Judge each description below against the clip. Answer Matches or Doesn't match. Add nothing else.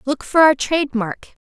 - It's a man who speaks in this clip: Doesn't match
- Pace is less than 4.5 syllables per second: Doesn't match